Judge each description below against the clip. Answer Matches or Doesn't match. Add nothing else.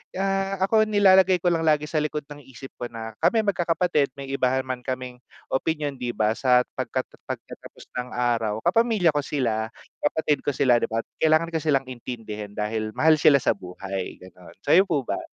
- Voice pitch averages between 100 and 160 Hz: Matches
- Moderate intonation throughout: Doesn't match